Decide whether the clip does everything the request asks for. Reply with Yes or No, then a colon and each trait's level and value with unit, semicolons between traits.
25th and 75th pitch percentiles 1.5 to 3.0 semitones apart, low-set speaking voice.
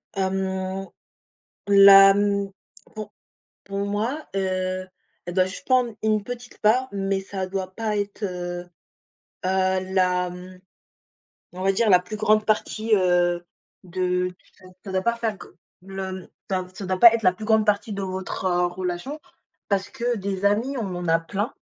No: narrow, 2.4 semitones; high, 195 Hz